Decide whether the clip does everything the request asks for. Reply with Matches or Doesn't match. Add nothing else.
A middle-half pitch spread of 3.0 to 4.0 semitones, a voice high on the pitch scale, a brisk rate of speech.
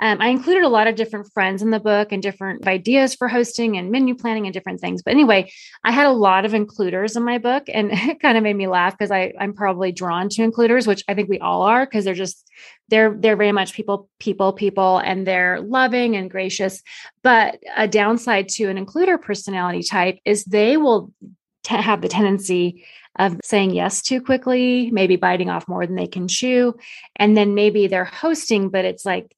Matches